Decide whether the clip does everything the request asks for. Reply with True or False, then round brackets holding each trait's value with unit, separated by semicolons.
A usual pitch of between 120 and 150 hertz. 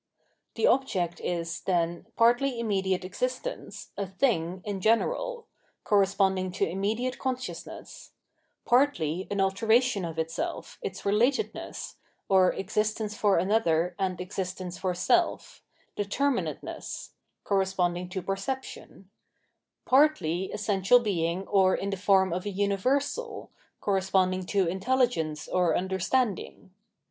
False (195 Hz)